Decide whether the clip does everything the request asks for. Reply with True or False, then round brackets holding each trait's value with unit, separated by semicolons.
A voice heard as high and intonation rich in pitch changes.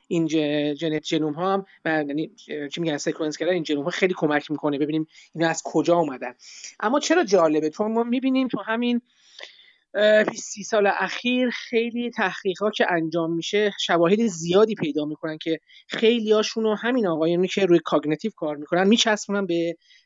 False (180 Hz; 5.7 semitones)